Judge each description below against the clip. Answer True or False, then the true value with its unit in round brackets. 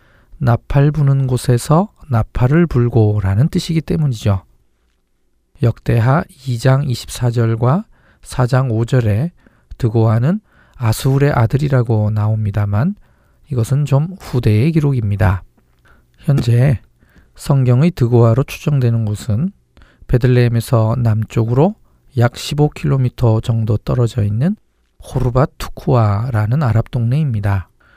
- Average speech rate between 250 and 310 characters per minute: False (235 characters per minute)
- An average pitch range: True (4.0 semitones)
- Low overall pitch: True (120 Hz)